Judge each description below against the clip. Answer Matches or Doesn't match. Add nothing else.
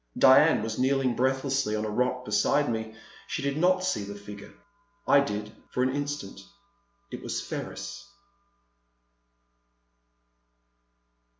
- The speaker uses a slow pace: Matches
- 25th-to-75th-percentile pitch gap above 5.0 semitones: Doesn't match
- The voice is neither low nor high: Doesn't match